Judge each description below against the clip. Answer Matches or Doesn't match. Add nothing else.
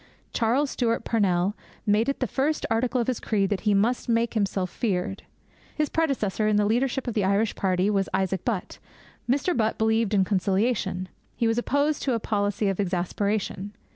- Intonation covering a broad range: Doesn't match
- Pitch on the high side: Matches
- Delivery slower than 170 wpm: Doesn't match